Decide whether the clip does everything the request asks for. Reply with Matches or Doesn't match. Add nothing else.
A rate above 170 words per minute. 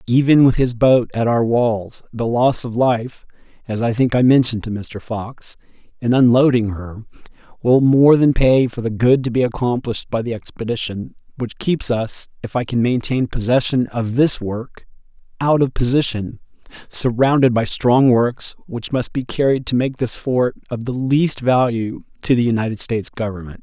Matches